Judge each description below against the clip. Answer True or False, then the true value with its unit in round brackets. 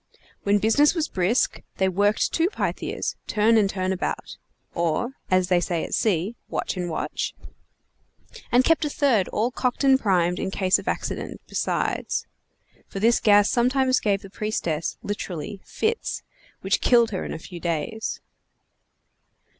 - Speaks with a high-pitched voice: True (205 Hz)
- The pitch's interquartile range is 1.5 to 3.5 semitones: False (4.6 semitones)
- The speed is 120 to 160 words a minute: True (155 wpm)